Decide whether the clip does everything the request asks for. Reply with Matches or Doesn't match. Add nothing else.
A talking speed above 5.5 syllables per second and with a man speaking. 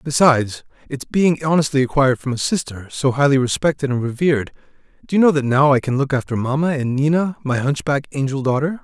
Matches